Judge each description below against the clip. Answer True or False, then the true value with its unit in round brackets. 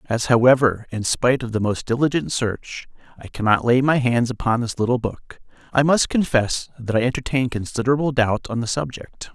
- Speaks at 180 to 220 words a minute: True (185 wpm)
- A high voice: False (120 Hz)